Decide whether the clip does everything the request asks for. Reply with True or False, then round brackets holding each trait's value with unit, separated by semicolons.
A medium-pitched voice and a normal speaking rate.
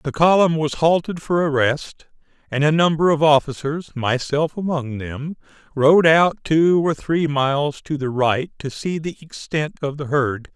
True (150 Hz; 175 wpm)